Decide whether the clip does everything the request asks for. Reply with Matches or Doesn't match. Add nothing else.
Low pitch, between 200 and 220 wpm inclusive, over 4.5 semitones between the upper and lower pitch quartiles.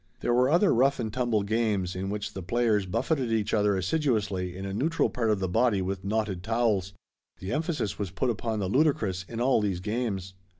Doesn't match